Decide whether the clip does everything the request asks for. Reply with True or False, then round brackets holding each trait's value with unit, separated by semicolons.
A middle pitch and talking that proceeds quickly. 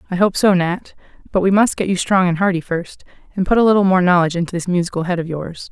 True (180 Hz; 265 wpm)